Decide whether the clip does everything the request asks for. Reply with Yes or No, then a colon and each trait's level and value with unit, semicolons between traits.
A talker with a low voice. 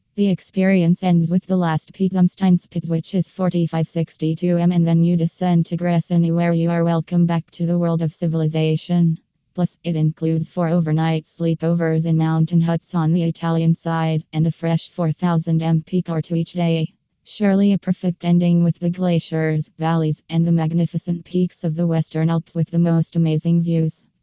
No: medium, 170 Hz